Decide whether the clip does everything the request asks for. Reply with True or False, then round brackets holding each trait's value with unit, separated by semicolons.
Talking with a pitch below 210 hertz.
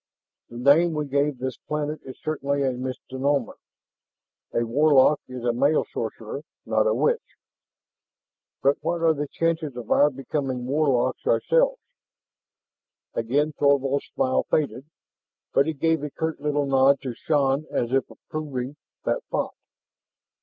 True (140 Hz)